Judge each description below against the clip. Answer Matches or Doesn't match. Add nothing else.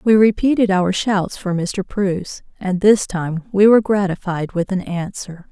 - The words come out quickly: Doesn't match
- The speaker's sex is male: Doesn't match